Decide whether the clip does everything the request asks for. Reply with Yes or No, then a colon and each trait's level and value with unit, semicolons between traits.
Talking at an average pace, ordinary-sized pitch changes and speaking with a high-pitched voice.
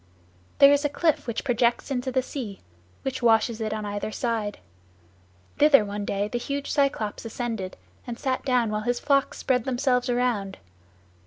Yes: average, 165 wpm; average, 3.7 semitones; high, 245 Hz